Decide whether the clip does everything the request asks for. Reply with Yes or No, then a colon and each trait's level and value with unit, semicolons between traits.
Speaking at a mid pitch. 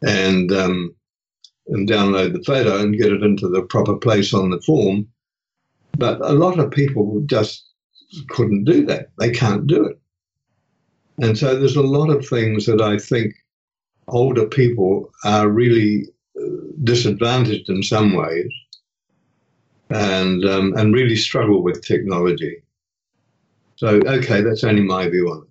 No: low, 110 Hz